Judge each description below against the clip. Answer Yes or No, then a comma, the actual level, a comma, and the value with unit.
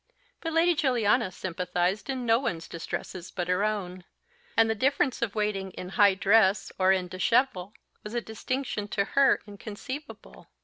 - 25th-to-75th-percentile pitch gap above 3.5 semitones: Yes, average, 4.7 semitones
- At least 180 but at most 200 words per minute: No, average, 160 wpm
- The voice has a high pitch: Yes, high, 210 Hz